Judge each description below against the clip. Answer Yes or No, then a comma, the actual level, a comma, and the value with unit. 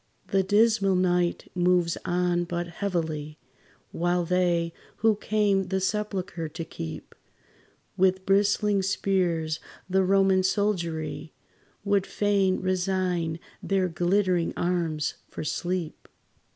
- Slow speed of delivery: Yes, slow, 105 wpm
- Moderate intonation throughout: No, narrow, 2.3 semitones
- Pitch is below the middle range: No, medium, 185 Hz